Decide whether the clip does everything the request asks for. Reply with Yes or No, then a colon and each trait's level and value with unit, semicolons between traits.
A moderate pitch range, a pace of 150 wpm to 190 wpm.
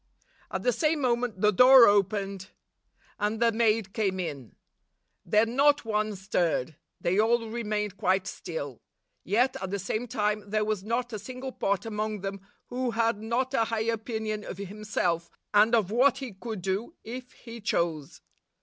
Yes: average, 3.1 semitones; average, 170 wpm